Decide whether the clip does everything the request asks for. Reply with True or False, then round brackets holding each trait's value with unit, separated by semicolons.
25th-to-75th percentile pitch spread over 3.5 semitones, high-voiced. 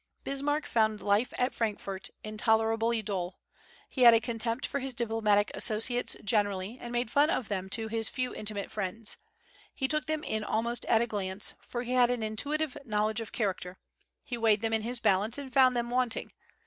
False (2.7 semitones; 225 Hz)